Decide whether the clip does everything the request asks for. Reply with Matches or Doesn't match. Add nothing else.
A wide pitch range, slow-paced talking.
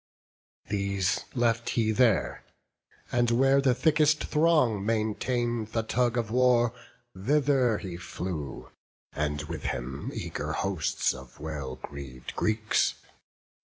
Matches